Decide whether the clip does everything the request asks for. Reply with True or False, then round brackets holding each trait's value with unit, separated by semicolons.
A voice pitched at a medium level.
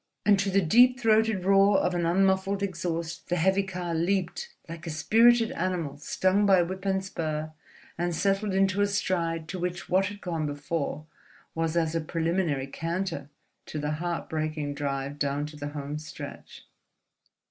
True (175 Hz)